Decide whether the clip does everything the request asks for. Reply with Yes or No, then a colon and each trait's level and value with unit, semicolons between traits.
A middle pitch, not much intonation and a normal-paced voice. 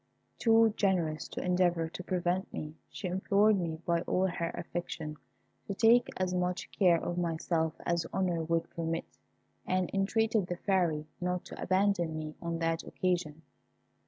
Yes: medium, 175 Hz; narrow, 2.3 semitones; average, 155 wpm